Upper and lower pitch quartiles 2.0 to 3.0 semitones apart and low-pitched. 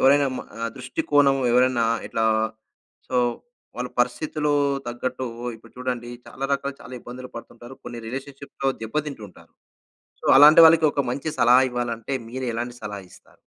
Yes: average, 2.7 semitones; low, 130 Hz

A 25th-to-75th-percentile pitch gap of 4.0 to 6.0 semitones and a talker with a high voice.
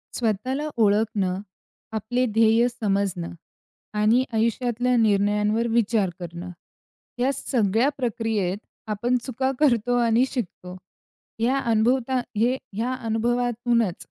No: average, 2.9 semitones; high, 225 Hz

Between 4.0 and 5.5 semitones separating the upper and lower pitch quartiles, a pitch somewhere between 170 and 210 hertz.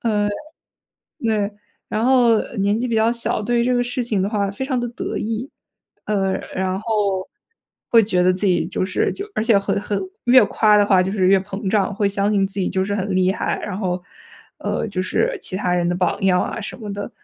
No: average, 3.0 semitones; high, 205 Hz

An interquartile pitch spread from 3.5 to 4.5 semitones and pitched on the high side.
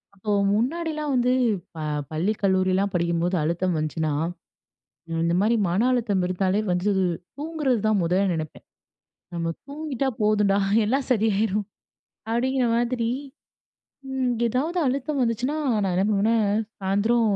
No: average, 5.3 semitones; high, 215 Hz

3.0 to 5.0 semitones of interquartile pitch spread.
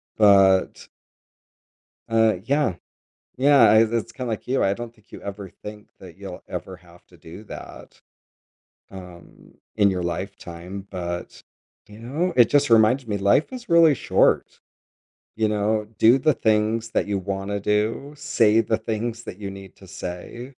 Yes: average, 3.4 semitones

